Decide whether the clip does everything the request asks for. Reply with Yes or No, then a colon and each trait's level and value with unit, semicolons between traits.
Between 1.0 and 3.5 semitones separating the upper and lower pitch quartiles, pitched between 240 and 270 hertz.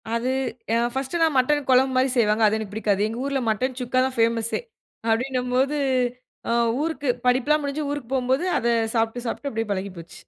Yes: average, 3.2 semitones; very high, 250 Hz